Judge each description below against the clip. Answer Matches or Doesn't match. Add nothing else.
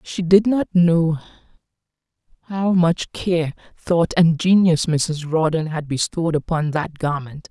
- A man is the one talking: Doesn't match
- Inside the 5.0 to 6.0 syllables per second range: Doesn't match